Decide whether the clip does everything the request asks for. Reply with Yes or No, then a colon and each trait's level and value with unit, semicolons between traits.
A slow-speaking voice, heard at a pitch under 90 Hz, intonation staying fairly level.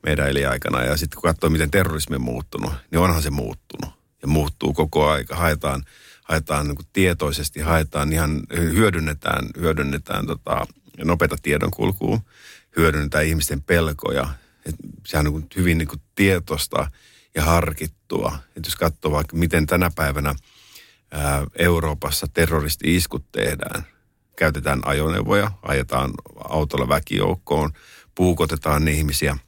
No: average, 125 wpm; very low, 75 Hz; narrow, 2.3 semitones